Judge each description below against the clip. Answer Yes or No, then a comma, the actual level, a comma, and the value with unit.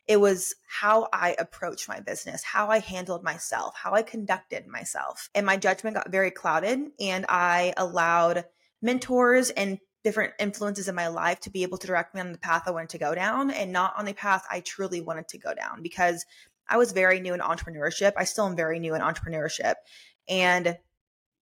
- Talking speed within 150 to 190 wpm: No, average, 200 wpm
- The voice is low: No, medium, 185 Hz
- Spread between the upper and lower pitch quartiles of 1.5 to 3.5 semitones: Yes, average, 2.8 semitones